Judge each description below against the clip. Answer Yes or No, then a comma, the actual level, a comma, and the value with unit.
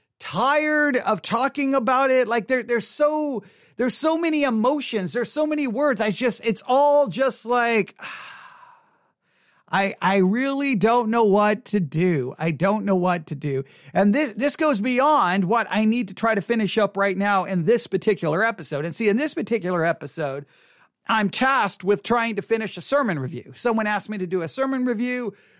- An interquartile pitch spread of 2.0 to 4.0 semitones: No, average, 5.3 semitones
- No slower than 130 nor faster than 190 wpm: Yes, average, 185 wpm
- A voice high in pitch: Yes, high, 225 Hz